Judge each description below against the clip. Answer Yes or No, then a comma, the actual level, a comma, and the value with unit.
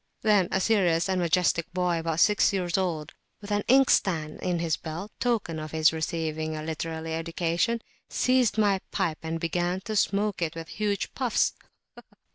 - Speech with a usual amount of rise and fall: Yes, average, 4.0 semitones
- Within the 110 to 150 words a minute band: No, average, 170 wpm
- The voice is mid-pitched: Yes, medium, 175 Hz